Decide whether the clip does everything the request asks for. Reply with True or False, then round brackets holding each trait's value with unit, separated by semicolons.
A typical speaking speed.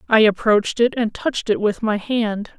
False (210 wpm)